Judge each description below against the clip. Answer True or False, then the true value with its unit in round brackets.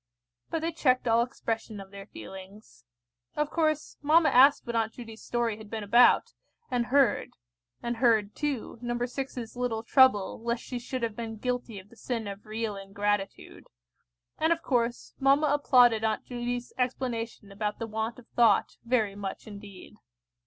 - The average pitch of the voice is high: True (235 Hz)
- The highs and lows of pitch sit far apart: False (2.8 semitones)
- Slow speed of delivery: False (165 wpm)